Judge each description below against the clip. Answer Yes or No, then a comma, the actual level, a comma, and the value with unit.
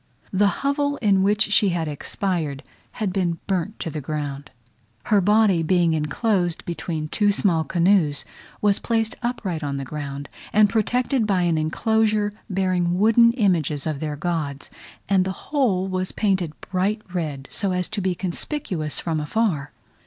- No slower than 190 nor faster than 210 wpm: No, average, 155 wpm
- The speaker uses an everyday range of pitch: Yes, average, 4.9 semitones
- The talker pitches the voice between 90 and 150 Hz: No, medium, 185 Hz